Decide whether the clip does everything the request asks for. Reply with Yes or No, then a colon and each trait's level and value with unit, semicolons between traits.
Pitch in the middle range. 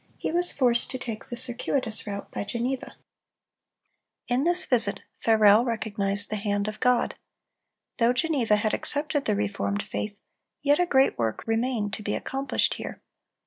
No: high, 230 Hz